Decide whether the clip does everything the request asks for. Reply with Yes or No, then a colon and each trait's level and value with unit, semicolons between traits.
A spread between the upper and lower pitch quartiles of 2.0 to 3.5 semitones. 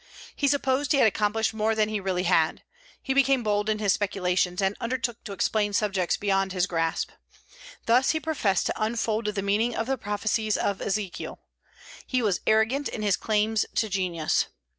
Yes: average, 2.9 semitones